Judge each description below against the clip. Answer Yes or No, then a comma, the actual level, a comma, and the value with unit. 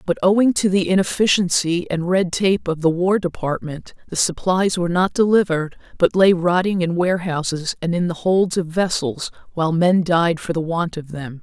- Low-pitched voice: No, medium, 175 Hz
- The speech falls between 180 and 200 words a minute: Yes, average, 190 wpm